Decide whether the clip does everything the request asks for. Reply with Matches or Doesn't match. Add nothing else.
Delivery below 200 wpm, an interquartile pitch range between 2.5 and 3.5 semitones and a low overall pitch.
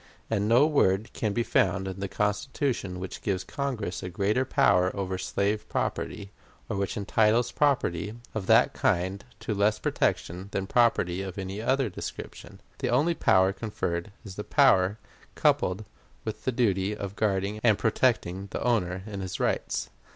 Matches